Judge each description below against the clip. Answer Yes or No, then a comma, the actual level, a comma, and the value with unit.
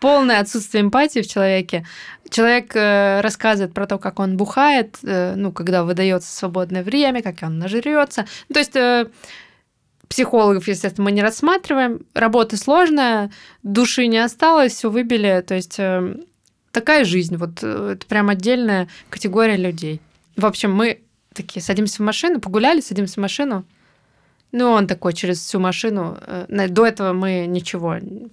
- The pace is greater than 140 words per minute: Yes, average, 155 wpm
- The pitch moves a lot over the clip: No, average, 4.1 semitones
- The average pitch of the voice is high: Yes, high, 205 Hz